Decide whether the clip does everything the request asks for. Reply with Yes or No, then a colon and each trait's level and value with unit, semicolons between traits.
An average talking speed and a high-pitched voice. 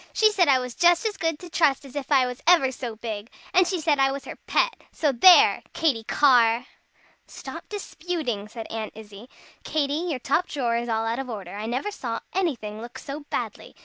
No: fast, 210 wpm; very high, 265 Hz